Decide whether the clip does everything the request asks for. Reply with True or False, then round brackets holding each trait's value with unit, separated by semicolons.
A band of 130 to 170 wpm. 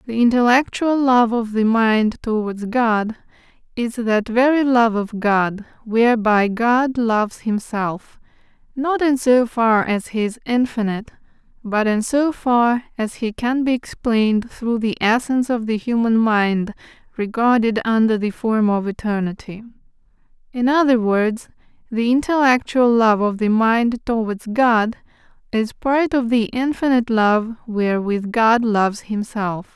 True (140 wpm)